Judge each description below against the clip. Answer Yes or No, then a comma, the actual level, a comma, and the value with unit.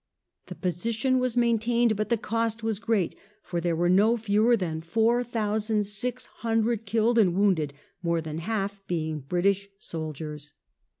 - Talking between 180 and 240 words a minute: No, average, 160 wpm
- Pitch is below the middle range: No, high, 210 Hz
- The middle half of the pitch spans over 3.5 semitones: Yes, average, 4.7 semitones